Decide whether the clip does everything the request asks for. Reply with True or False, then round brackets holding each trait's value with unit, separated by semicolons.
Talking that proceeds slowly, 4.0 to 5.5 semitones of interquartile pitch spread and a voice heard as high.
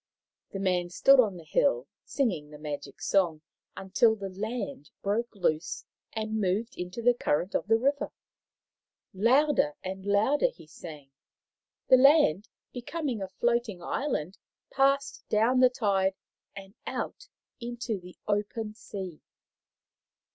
True (130 wpm; 5.0 semitones; 210 Hz)